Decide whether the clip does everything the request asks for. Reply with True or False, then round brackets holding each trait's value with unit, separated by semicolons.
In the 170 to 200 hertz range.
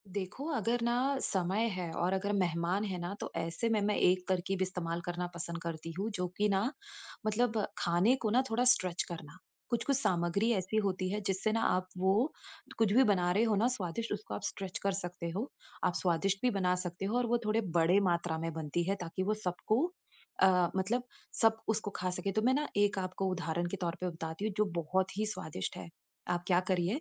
True (190 Hz)